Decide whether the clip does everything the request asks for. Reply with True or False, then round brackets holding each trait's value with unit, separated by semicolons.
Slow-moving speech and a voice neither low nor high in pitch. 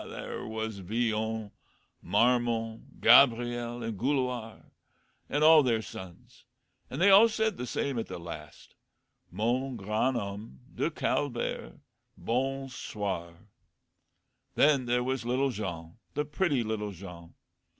False (120 wpm; 120 Hz)